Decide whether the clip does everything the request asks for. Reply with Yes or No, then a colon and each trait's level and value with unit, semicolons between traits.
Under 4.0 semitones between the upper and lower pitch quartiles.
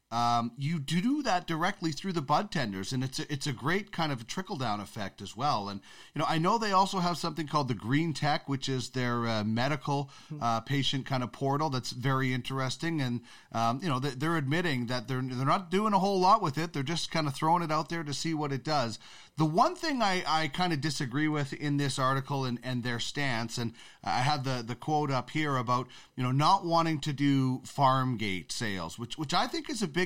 No: average, 4.5 semitones